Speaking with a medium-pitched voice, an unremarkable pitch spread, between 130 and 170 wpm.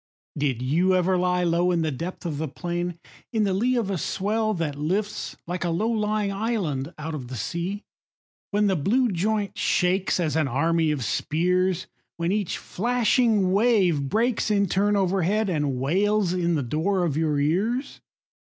No: medium, 180 Hz; average, 4.4 semitones; average, 180 wpm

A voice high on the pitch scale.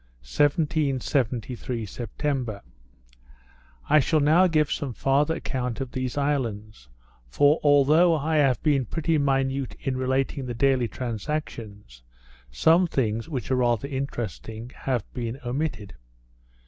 No: low, 130 Hz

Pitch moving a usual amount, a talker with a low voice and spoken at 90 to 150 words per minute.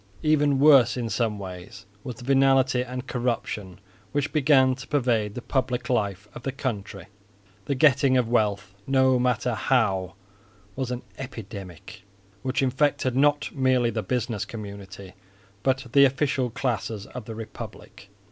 Yes: average, 4.0 semitones; low, 125 Hz; average, 145 wpm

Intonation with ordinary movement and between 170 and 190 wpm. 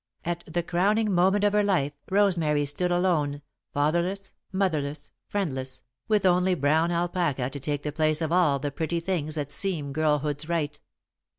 No: average, 3.9 semitones; average, 160 wpm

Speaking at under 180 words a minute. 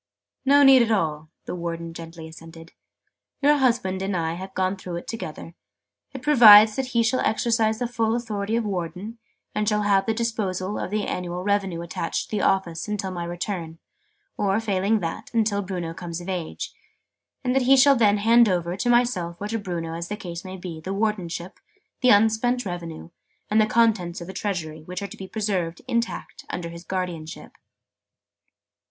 No: average, 185 wpm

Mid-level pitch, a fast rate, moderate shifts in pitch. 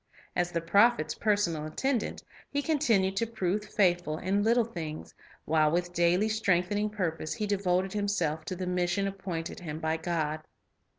No: medium, 180 Hz; average, 155 wpm; average, 3.9 semitones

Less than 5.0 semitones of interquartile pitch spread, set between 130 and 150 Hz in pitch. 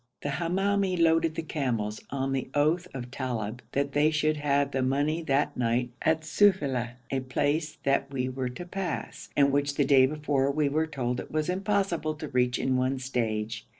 Yes: average, 3.4 semitones; medium, 140 Hz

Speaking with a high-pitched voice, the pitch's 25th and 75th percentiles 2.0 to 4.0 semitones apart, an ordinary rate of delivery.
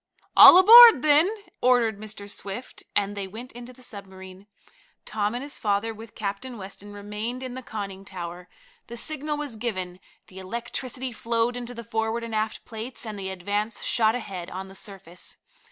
Yes: high, 220 Hz; average, 3.6 semitones; average, 170 wpm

